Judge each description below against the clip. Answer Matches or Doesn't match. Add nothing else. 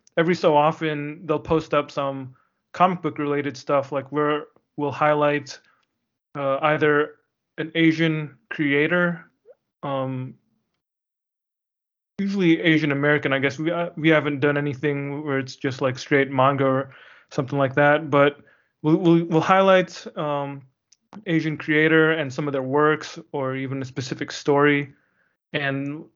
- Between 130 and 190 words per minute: Matches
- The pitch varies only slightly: Matches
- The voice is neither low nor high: Matches